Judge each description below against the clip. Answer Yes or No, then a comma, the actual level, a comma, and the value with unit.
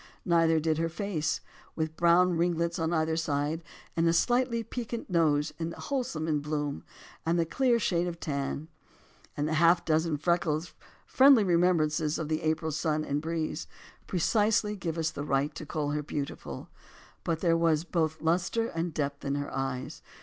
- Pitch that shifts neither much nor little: No, narrow, 2.1 semitones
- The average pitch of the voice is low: No, medium, 165 Hz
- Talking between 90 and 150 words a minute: No, average, 175 wpm